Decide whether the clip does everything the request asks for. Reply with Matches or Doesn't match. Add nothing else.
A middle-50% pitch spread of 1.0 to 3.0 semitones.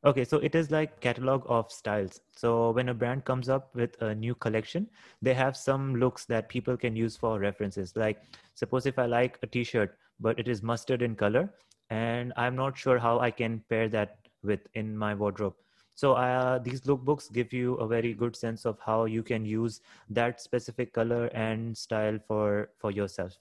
Matches